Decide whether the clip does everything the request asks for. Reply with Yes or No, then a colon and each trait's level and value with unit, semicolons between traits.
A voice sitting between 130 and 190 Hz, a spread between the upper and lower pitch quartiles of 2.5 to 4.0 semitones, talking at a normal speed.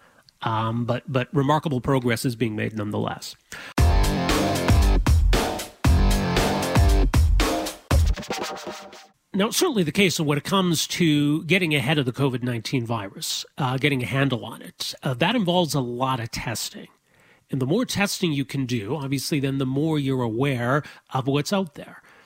No: low, 135 Hz; average, 4.4 semitones; average, 150 wpm